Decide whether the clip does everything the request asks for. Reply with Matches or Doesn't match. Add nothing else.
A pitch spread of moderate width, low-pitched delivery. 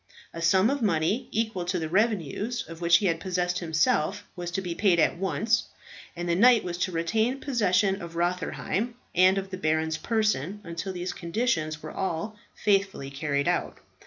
Doesn't match